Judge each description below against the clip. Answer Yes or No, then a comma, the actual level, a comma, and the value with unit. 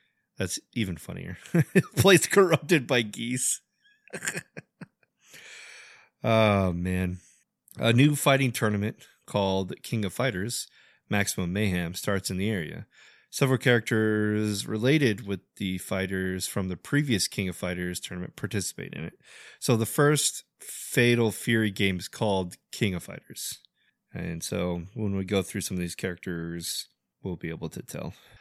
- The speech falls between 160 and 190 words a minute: No, slow, 135 wpm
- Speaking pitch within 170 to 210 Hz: No, low, 105 Hz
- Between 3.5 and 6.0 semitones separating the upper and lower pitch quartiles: Yes, average, 4.4 semitones